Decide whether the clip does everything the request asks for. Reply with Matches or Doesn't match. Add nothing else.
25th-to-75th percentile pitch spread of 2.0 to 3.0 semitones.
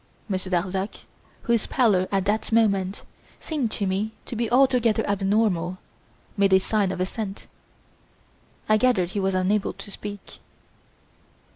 Matches